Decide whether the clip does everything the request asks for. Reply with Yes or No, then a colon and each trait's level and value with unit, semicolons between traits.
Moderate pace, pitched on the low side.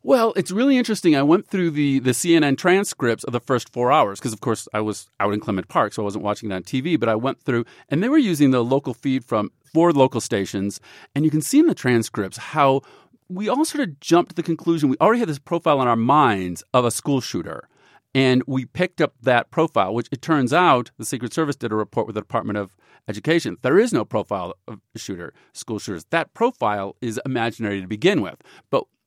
No: fast, 235 wpm; low, 130 Hz